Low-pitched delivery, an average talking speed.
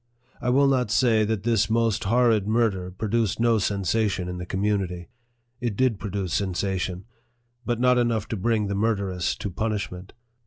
Yes: low, 105 Hz; average, 160 wpm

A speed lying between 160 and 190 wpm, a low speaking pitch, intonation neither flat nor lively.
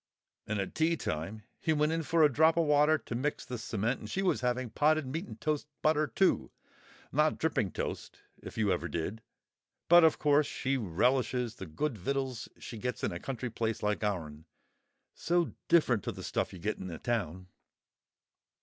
No: average, 185 wpm; low, 125 Hz; wide, 6.5 semitones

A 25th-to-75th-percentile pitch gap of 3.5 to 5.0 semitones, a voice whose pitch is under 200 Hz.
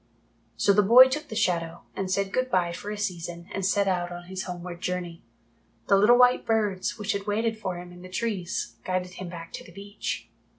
No: average, 3.0 semitones; high, 190 Hz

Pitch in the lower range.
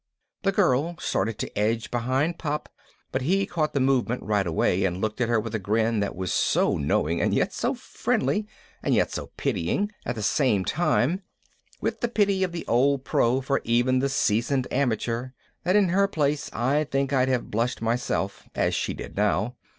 Yes: low, 130 Hz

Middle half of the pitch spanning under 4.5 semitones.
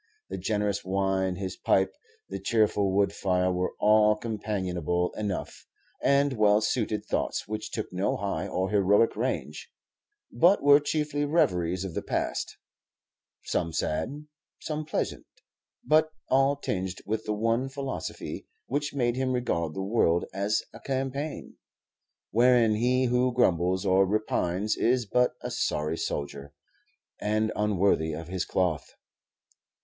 No: average, 5.1 semitones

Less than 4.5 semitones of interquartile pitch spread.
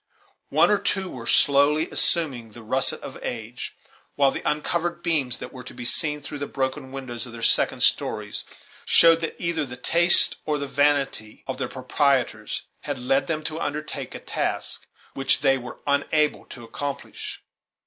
Yes: average, 3.3 semitones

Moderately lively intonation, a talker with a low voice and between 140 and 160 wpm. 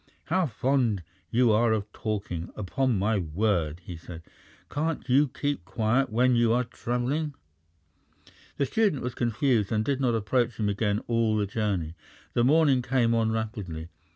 Yes: average, 3.9 semitones; low, 115 Hz; average, 155 wpm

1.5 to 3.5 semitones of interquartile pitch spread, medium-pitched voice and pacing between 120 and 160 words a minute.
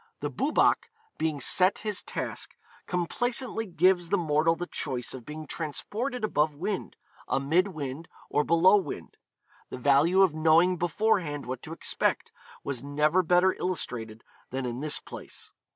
No: average, 4.3 semitones; medium, 165 Hz; average, 145 wpm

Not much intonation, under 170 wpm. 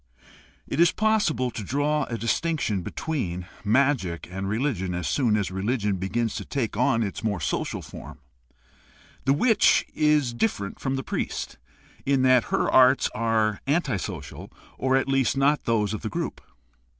No: average, 5.2 semitones; average, 160 wpm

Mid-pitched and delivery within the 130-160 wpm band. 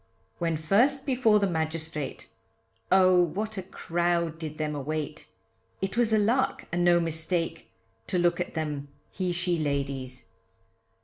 Yes: medium, 170 Hz; average, 140 wpm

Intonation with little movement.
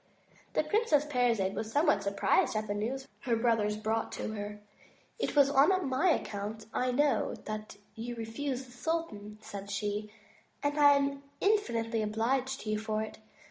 No: average, 4.6 semitones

